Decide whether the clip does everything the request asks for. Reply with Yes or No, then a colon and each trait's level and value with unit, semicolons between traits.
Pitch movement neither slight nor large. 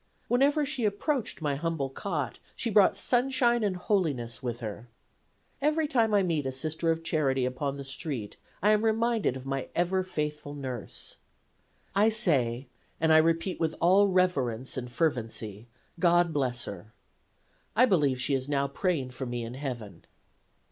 No: wide, 7.4 semitones